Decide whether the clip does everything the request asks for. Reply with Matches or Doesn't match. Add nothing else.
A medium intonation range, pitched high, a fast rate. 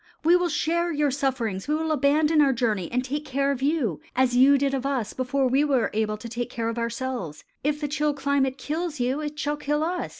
Matches